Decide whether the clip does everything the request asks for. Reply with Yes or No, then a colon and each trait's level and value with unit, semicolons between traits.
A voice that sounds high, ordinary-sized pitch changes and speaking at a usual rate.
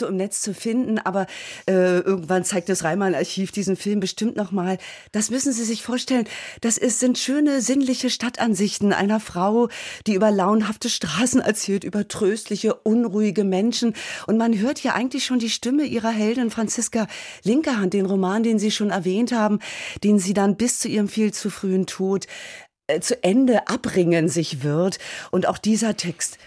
Yes: high, 215 Hz; average, 3.6 semitones; average, 175 wpm